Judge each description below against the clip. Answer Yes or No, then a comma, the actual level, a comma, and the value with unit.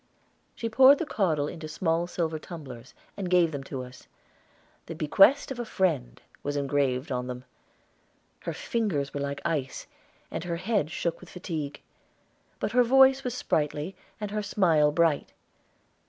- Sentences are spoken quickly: No, average, 155 wpm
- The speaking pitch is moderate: Yes, medium, 165 Hz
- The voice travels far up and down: Yes, wide, 5.9 semitones